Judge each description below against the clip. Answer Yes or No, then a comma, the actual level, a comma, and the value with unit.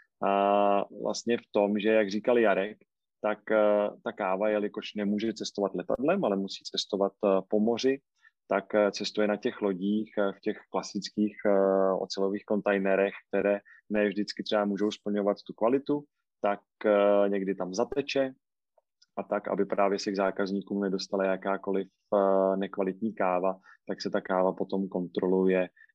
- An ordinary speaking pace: Yes, average, 155 wpm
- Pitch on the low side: Yes, low, 100 Hz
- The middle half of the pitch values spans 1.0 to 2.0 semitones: Yes, narrow, 1.4 semitones